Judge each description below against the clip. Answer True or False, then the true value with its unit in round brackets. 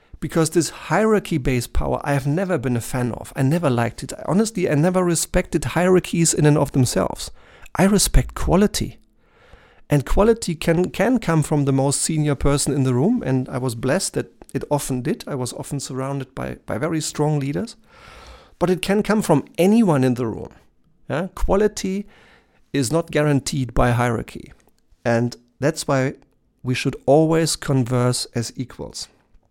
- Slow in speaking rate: False (170 wpm)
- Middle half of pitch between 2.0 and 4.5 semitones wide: False (5.0 semitones)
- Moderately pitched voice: True (145 Hz)